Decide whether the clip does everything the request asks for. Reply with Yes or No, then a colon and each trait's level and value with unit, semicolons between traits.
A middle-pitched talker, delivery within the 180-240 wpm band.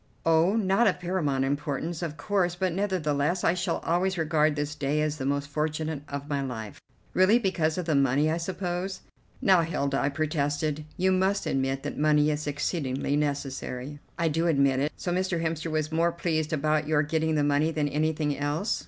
Yes: medium, 155 Hz; average, 190 wpm